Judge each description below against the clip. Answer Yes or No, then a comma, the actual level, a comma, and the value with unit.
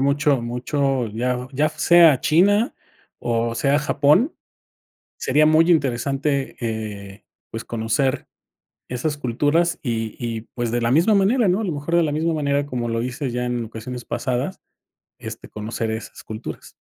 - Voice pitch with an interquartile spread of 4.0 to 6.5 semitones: Yes, average, 4.6 semitones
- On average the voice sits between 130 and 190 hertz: Yes, low, 135 Hz